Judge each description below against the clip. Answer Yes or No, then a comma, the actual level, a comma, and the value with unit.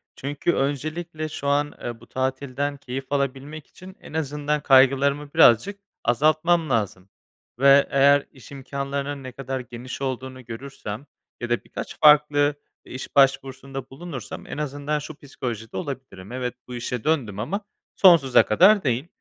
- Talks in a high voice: No, medium, 140 Hz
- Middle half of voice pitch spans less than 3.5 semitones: Yes, narrow, 2.5 semitones